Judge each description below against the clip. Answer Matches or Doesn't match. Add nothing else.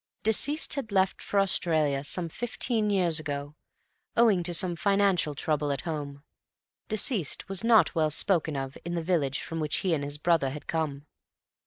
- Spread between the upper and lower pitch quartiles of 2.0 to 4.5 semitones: Doesn't match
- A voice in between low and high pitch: Matches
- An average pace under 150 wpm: Doesn't match